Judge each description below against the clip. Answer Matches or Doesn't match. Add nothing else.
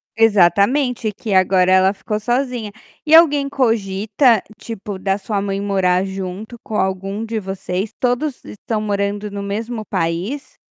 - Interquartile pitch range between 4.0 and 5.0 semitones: Doesn't match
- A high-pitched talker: Matches